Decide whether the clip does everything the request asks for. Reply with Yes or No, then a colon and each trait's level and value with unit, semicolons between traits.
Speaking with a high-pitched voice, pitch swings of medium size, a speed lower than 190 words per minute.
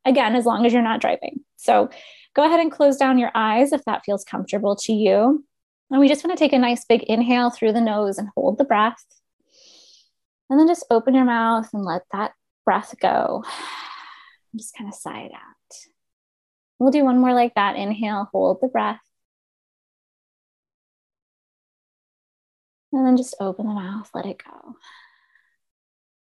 Yes: high, 235 Hz; average, 4.1 semitones; average, 170 wpm